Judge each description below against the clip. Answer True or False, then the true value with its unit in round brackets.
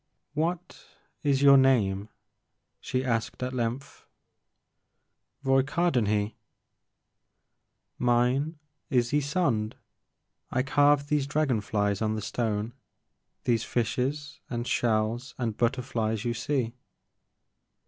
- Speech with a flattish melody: False (3.8 semitones)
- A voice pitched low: True (125 Hz)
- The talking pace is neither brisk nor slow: False (95 wpm)